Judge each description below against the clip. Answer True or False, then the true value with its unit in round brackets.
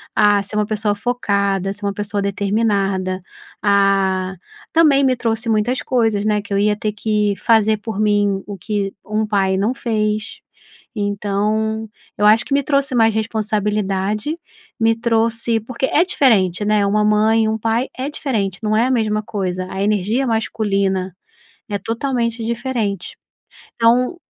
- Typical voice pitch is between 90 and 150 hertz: False (215 Hz)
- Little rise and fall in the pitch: True (2.2 semitones)